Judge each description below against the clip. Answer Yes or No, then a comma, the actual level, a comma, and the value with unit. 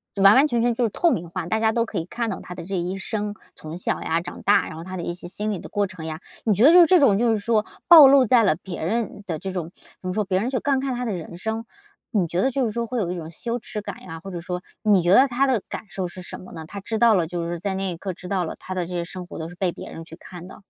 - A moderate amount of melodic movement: Yes, average, 4.7 semitones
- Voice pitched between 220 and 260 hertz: No, high, 195 Hz